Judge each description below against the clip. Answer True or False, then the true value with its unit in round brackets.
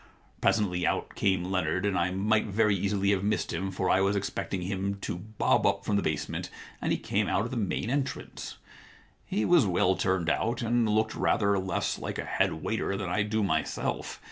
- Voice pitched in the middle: False (100 Hz)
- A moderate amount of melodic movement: False (2.3 semitones)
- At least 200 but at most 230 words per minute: True (205 wpm)